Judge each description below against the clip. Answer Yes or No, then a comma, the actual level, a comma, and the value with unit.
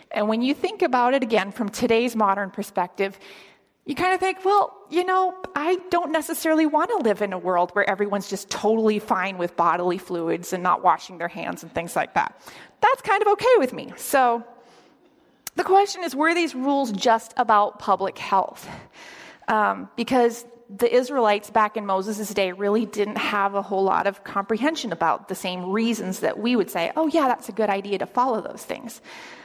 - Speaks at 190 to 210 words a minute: Yes, average, 195 wpm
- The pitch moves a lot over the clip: Yes, wide, 7.4 semitones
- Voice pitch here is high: Yes, high, 230 Hz